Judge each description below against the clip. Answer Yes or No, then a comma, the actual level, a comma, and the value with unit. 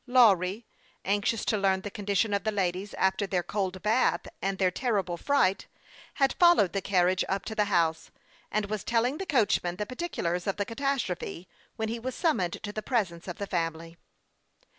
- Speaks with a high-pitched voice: Yes, high, 200 Hz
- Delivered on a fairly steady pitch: No, average, 3.8 semitones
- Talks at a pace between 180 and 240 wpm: Yes, average, 185 wpm